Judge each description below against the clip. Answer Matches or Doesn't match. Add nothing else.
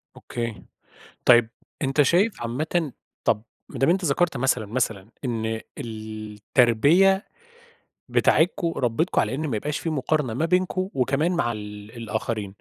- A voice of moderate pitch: Doesn't match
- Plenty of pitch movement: Matches